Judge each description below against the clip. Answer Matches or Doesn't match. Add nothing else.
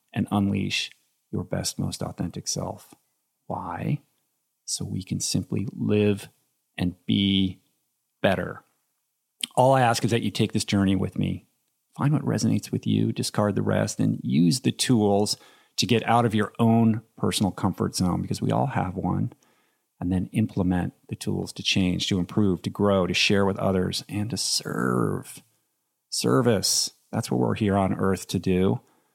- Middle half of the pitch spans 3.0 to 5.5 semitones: Doesn't match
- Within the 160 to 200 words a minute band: Matches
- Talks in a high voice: Doesn't match